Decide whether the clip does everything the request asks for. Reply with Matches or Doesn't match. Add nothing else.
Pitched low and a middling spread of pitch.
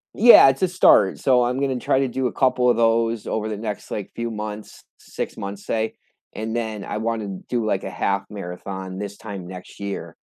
Matches